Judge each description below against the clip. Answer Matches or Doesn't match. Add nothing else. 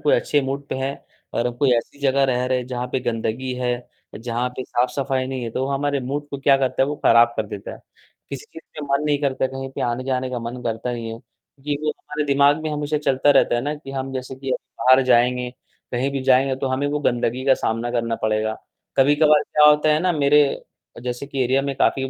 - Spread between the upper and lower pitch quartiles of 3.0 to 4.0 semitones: Doesn't match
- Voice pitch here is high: Doesn't match